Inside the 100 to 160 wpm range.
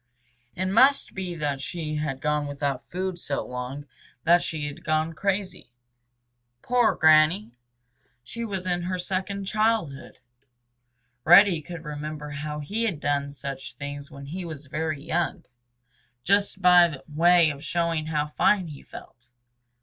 Yes: average, 140 wpm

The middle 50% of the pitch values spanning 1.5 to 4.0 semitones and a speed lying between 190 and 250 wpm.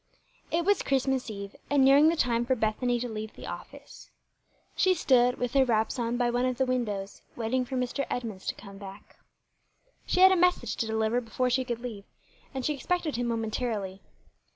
Yes: average, 3.1 semitones; average, 195 wpm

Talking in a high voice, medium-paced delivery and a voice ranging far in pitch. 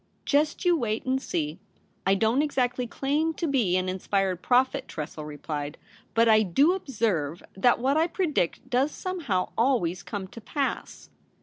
Yes: high, 235 Hz; average, 175 wpm; wide, 7.2 semitones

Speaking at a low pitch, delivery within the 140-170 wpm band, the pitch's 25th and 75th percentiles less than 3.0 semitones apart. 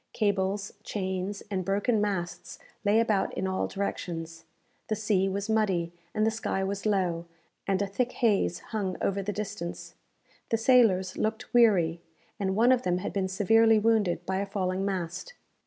No: high, 200 Hz; average, 165 wpm; narrow, 2.6 semitones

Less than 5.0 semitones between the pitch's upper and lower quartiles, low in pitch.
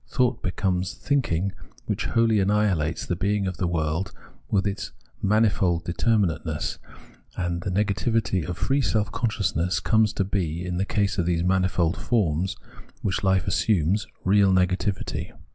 Yes: average, 3.0 semitones; very low, 95 Hz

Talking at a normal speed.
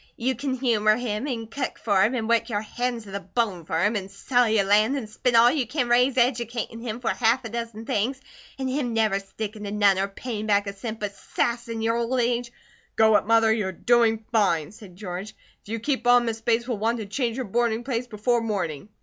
No: fast, 235 wpm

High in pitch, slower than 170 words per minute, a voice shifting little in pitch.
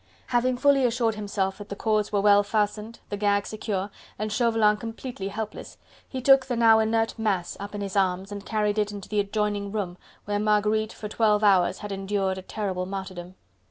No: high, 210 Hz; average, 195 wpm; narrow, 1.7 semitones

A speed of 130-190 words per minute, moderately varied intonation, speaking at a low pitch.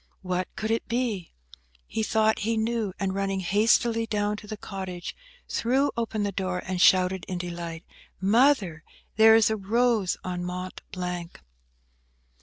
No: average, 150 wpm; average, 3.5 semitones; high, 200 Hz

